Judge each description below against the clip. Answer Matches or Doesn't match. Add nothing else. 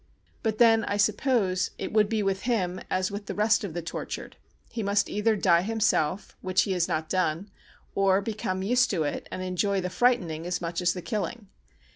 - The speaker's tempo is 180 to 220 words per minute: Matches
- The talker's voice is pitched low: Doesn't match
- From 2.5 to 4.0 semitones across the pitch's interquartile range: Matches